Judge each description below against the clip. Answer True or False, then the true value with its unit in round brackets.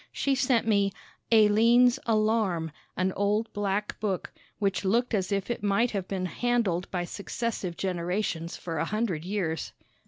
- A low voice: False (200 Hz)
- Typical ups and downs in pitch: True (3.6 semitones)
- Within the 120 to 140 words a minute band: False (150 wpm)